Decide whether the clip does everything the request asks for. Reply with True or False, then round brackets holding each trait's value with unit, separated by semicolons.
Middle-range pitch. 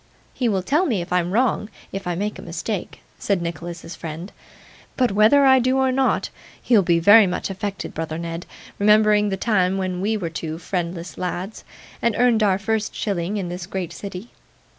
False (195 Hz)